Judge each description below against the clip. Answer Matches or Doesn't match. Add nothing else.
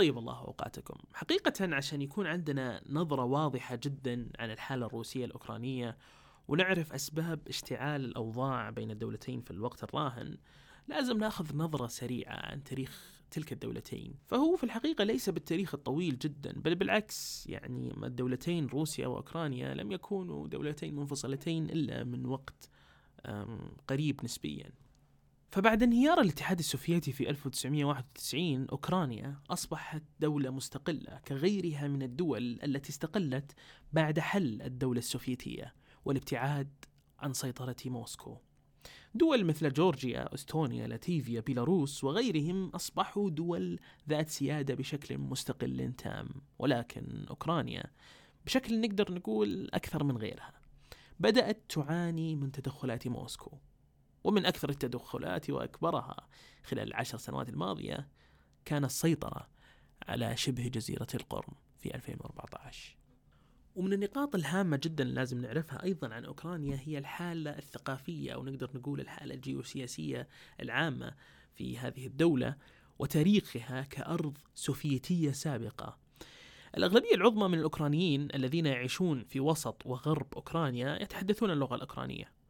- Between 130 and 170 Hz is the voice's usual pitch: Matches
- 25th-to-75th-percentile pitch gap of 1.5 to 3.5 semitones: Doesn't match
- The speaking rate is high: Doesn't match